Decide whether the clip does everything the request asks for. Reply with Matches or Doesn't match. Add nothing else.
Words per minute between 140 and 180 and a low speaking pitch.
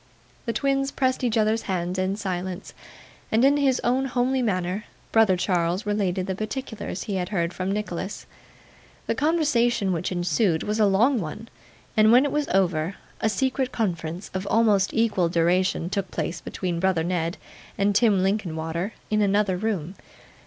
Doesn't match